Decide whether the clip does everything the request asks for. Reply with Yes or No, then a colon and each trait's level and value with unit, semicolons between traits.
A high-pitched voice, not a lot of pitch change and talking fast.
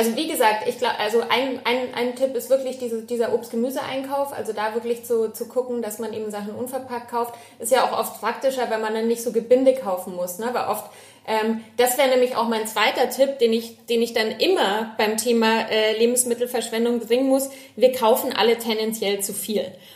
Yes: high, 235 Hz; narrow, 2.3 semitones; fast, 210 wpm